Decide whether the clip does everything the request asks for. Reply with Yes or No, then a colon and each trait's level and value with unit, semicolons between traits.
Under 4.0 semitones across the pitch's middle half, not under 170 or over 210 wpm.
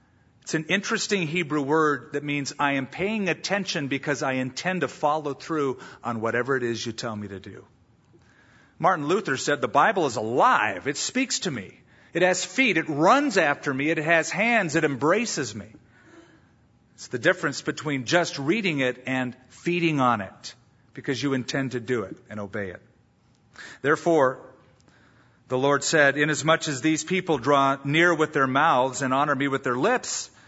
No: average, 4.3 semitones; average, 175 wpm